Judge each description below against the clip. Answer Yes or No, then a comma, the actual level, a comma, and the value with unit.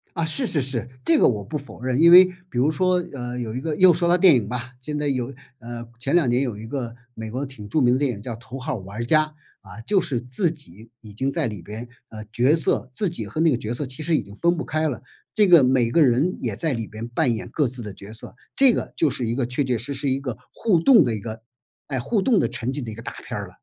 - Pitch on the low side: Yes, low, 130 Hz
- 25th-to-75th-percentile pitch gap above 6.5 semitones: No, average, 5.2 semitones